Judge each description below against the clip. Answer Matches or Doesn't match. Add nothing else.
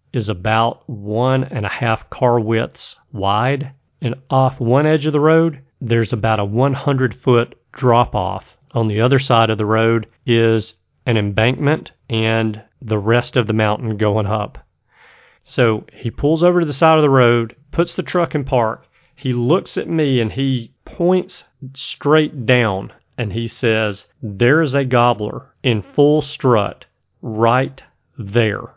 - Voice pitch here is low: Matches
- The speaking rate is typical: Matches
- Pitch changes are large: Doesn't match